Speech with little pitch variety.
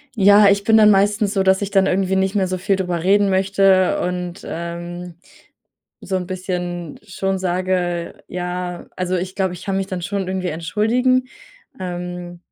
Yes: narrow, 1.7 semitones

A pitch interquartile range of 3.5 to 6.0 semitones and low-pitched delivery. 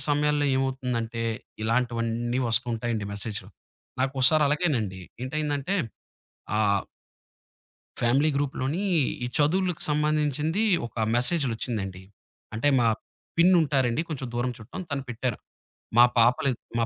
Yes: average, 4.3 semitones; low, 130 Hz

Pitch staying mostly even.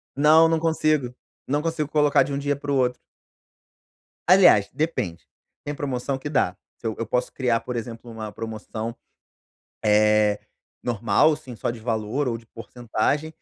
No: average, 4.7 semitones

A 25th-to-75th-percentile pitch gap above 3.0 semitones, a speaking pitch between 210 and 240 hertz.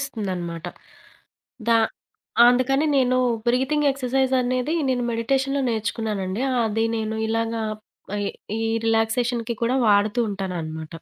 Yes: average, 3.5 semitones; high, 230 Hz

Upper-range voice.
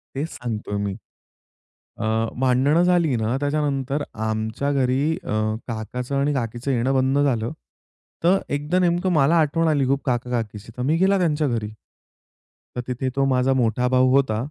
No: low, 135 Hz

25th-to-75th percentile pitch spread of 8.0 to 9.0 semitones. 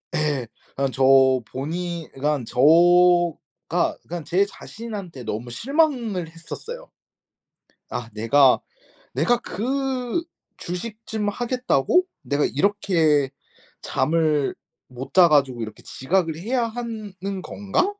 Yes: wide, 8.6 semitones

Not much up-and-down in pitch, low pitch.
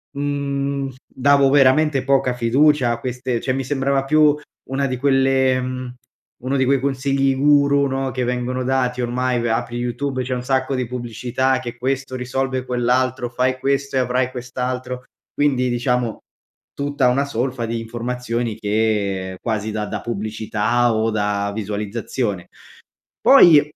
Yes: narrow, 2.2 semitones; low, 125 Hz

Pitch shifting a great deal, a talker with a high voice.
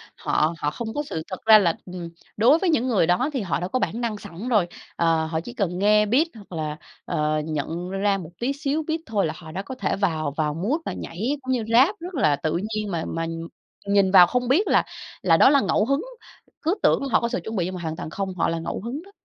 Yes: wide, 7.0 semitones; high, 200 Hz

